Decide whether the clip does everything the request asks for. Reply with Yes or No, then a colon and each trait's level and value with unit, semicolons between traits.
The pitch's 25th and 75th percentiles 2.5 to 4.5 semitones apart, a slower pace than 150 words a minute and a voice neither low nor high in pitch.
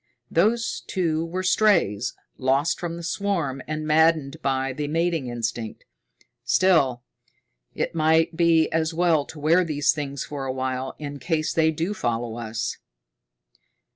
Yes: average, 4.0 semitones; average, 140 wpm; medium, 155 Hz